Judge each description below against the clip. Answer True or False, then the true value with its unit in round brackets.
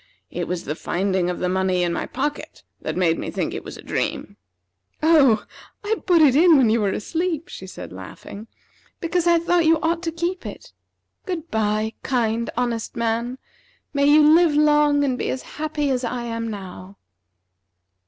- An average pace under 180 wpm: False (185 wpm)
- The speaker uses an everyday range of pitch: False (6.9 semitones)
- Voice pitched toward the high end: True (260 Hz)